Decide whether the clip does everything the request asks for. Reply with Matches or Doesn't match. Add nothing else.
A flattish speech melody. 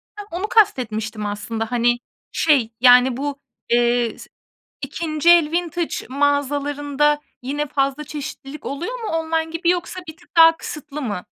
Doesn't match